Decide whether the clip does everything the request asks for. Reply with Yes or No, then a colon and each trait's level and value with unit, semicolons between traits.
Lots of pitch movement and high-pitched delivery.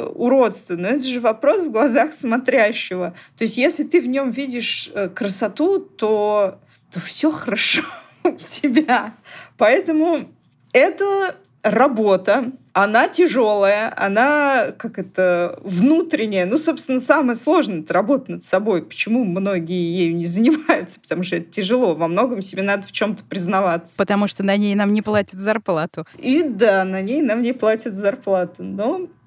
Yes: wide, 6.8 semitones; high, 225 Hz